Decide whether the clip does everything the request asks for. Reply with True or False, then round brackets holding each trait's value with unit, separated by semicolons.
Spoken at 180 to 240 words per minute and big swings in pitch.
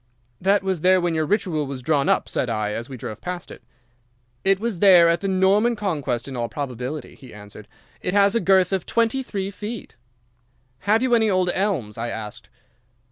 True (195 wpm; 7.0 semitones)